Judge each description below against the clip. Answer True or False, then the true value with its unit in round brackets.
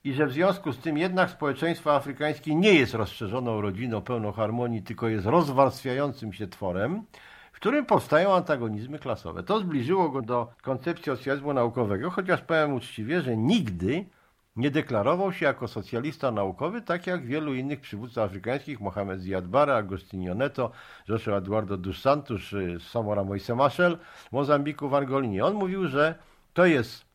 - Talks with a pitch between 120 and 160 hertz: True (135 Hz)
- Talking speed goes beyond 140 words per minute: True (150 wpm)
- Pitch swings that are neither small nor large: False (6.1 semitones)